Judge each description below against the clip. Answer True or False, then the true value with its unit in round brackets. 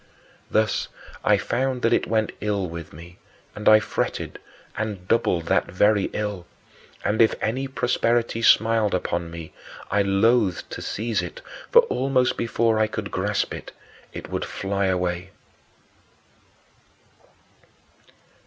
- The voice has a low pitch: True (105 Hz)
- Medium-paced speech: False (130 wpm)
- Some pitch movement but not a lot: True (3.7 semitones)